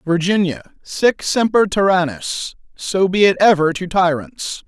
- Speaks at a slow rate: Yes, slow, 115 wpm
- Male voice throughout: Yes, male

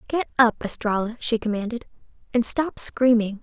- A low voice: No, high, 235 Hz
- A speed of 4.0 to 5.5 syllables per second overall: Yes, 4.9 syllables/s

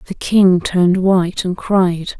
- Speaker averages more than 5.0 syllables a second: No, 4.0 syllables/s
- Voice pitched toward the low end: No, medium, 185 Hz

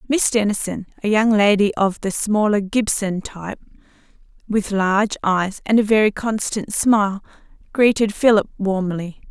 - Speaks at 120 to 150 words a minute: Yes, slow, 135 wpm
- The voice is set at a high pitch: Yes, high, 205 Hz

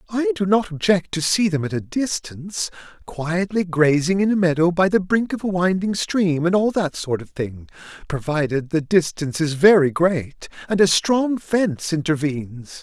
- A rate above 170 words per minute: Yes, average, 180 wpm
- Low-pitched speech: No, medium, 175 Hz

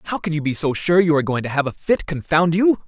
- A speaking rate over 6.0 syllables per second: Yes, 6.5 syllables/s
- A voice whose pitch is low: No, medium, 160 Hz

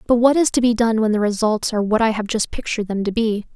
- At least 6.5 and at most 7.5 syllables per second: Yes, 6.6 syllables/s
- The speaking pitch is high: Yes, high, 220 Hz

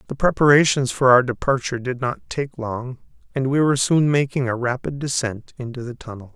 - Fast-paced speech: No, average, 190 wpm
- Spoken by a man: Yes, male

